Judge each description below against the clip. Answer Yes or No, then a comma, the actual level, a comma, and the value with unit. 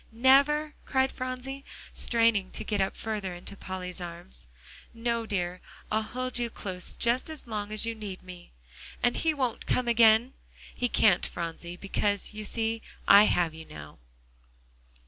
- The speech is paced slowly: No, average, 155 wpm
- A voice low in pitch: No, high, 220 Hz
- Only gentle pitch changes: No, average, 4.7 semitones